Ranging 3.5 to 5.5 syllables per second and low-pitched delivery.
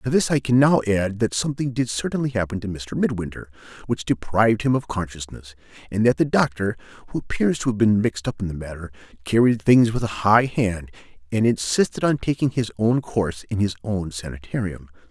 No: 5.7 syllables/s; low, 105 Hz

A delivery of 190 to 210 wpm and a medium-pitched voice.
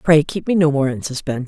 No: fast, 285 wpm; medium, 145 Hz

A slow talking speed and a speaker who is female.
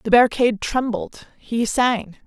Yes: slow, 130 wpm; female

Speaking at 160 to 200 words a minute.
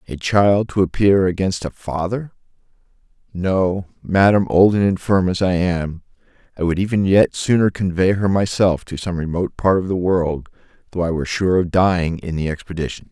Yes: average, 175 wpm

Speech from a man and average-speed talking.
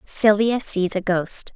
No: female; average, 155 wpm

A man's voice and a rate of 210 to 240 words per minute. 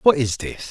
No: male; fast, 255 wpm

